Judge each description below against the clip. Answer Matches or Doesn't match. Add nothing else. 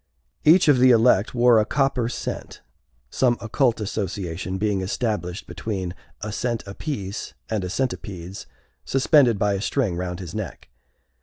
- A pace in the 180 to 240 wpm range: Doesn't match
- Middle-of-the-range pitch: Doesn't match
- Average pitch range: Matches